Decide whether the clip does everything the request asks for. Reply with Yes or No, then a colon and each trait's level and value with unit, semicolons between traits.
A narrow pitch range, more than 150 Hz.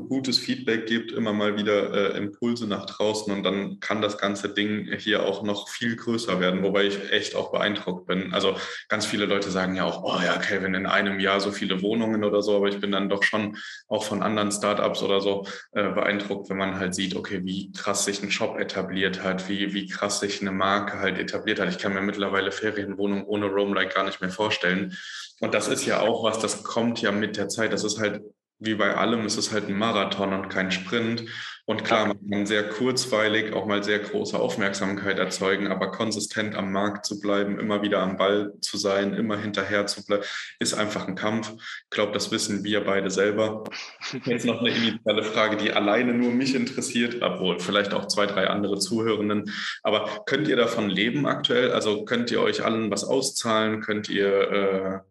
No: narrow, 1.4 semitones; low, 100 Hz